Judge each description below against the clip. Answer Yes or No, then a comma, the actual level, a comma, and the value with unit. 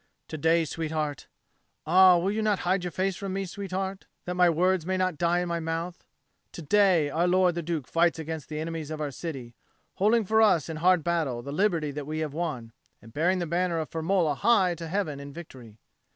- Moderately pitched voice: Yes, medium, 170 Hz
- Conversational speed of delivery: No, fast, 215 wpm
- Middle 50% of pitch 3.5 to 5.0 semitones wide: No, average, 3.1 semitones